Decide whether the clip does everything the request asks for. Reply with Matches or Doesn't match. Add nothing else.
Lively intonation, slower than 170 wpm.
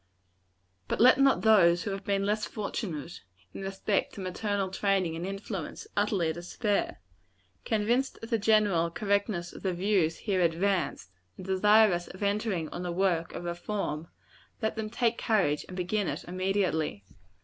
Doesn't match